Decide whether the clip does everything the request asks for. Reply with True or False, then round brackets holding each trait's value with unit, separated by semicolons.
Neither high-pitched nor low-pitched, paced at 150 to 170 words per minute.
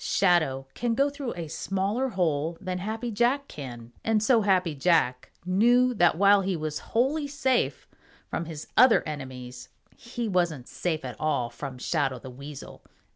True (180 Hz; 160 wpm)